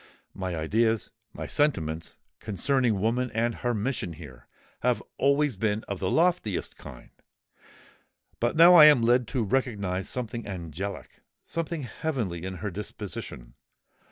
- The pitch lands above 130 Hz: No, low, 110 Hz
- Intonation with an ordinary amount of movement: No, wide, 5.7 semitones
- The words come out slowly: Yes, slow, 125 wpm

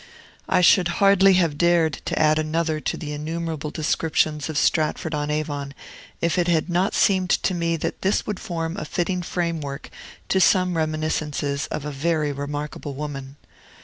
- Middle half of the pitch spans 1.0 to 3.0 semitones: Yes, average, 2.7 semitones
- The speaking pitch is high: No, medium, 160 Hz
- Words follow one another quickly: No, average, 165 wpm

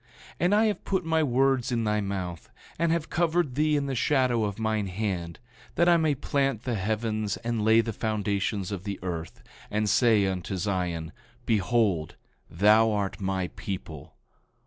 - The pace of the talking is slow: No, average, 170 wpm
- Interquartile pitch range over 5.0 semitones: Yes, wide, 5.5 semitones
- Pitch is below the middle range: Yes, low, 110 Hz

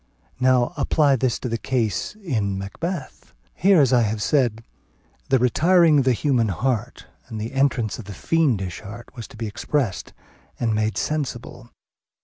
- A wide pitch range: No, average, 4.4 semitones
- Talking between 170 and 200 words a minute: No, average, 160 wpm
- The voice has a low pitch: Yes, low, 120 Hz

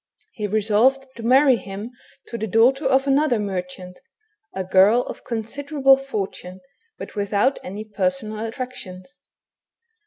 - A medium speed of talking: No, slow, 125 wpm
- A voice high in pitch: Yes, high, 220 Hz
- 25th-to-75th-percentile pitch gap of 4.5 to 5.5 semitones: Yes, average, 5.1 semitones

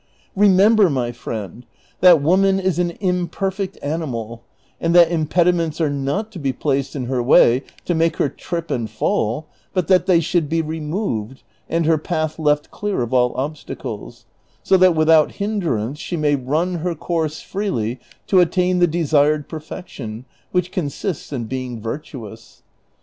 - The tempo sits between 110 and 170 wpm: Yes, average, 160 wpm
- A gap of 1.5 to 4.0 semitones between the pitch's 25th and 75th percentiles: No, average, 5.0 semitones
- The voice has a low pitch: No, medium, 155 Hz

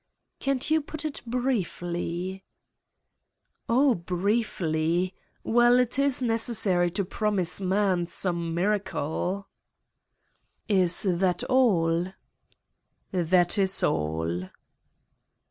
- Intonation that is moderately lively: Yes, average, 5.0 semitones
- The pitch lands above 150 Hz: Yes, high, 190 Hz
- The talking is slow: Yes, slow, 85 wpm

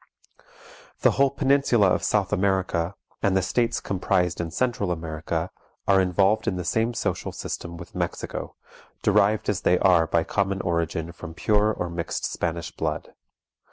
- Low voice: Yes, very low, 95 Hz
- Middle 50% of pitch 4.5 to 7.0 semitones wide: No, average, 3.6 semitones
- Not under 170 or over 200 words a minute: No, average, 155 wpm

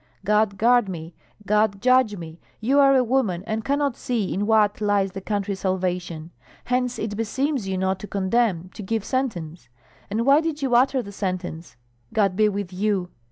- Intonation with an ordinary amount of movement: Yes, average, 4.4 semitones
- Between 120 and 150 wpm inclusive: No, average, 180 wpm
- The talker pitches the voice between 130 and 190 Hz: No, high, 210 Hz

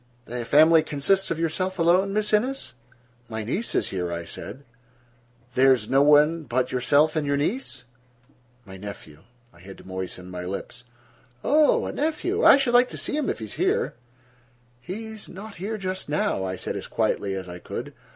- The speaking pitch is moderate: Yes, medium, 150 Hz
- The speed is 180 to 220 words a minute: Yes, average, 190 wpm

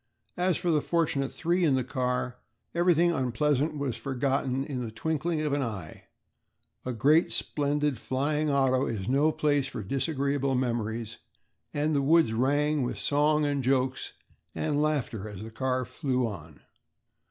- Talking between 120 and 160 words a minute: Yes, average, 155 wpm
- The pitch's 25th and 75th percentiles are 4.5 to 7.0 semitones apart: No, average, 3.1 semitones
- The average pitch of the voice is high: No, low, 135 Hz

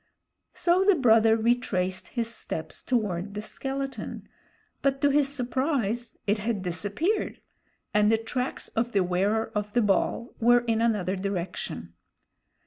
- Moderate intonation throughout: Yes, average, 4.0 semitones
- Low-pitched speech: No, high, 225 Hz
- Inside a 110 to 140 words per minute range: Yes, slow, 135 wpm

